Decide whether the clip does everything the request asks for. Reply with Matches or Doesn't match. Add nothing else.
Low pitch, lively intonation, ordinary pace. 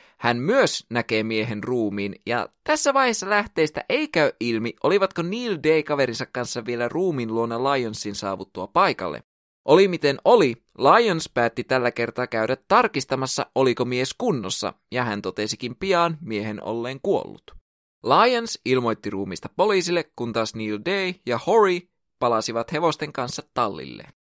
Matches